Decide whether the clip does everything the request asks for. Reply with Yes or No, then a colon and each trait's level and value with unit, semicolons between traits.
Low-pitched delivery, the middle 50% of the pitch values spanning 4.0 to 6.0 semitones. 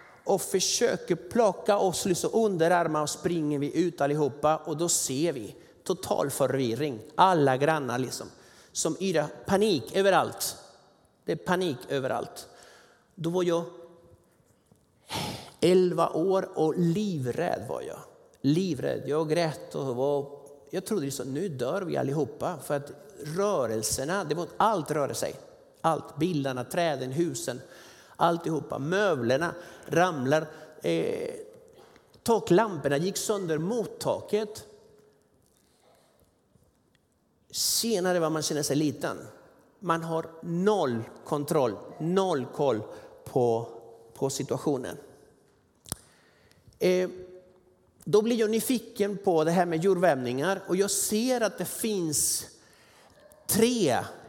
No: medium, 170 Hz; average, 5.2 semitones